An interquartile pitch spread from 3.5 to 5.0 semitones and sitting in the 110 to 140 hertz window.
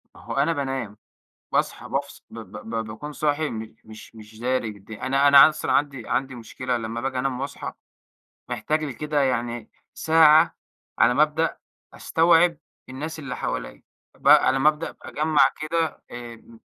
Yes: average, 4.6 semitones; low, 135 Hz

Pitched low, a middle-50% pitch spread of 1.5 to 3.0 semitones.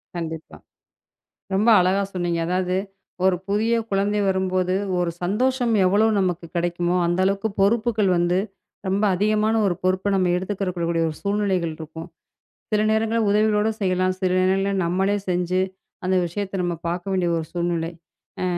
No: medium, 185 Hz; average, 2.7 semitones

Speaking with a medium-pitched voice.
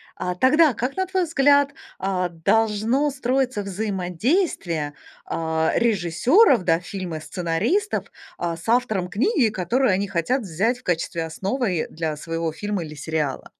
No: high, 195 Hz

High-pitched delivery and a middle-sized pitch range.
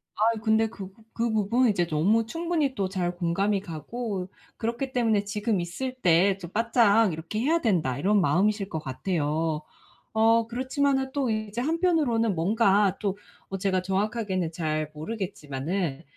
Yes: high, 205 Hz; average, 4.6 semitones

